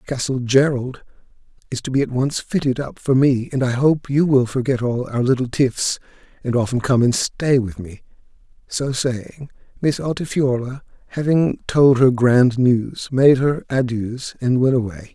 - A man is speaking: Yes, male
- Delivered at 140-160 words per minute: No, average, 170 wpm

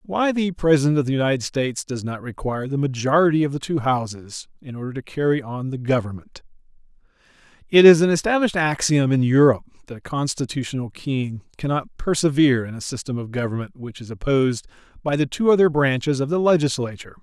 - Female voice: No, male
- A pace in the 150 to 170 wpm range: No, average, 180 wpm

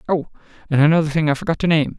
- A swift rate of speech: Yes, fast, 240 wpm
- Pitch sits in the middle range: Yes, medium, 155 Hz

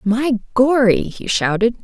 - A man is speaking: No, female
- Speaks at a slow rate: Yes, slow, 130 wpm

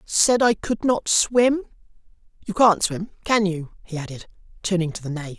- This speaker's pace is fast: No, average, 180 wpm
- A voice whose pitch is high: Yes, high, 195 Hz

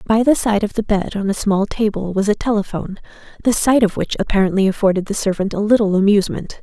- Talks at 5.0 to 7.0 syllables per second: Yes, 6.3 syllables/s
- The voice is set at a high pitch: Yes, high, 205 Hz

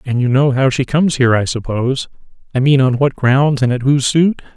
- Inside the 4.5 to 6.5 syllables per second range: Yes, 5.9 syllables/s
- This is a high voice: No, low, 135 Hz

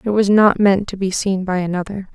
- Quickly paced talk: Yes, fast, 250 wpm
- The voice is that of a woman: Yes, female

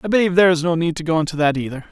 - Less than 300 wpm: No, fast, 345 wpm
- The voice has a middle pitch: Yes, medium, 165 Hz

